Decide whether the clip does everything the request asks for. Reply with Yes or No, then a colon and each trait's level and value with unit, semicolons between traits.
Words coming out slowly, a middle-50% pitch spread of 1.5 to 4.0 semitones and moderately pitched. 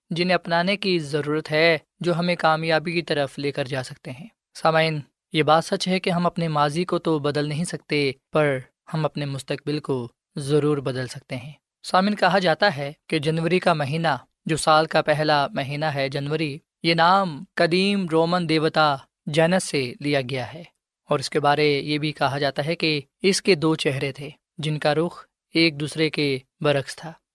No: fast, 190 wpm; average, 2.8 semitones; medium, 155 Hz